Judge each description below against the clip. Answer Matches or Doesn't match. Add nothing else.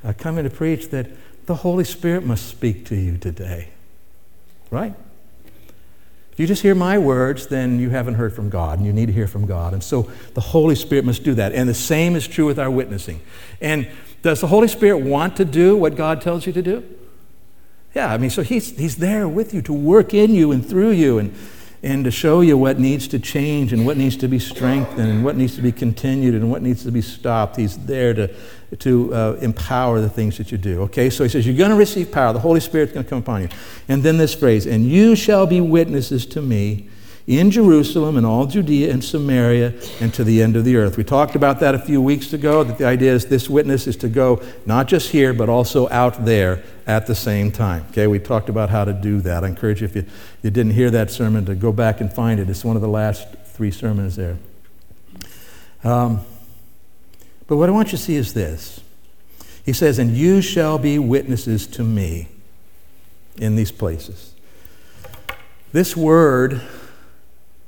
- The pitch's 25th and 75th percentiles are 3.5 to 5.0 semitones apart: Doesn't match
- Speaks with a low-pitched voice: Matches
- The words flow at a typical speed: Doesn't match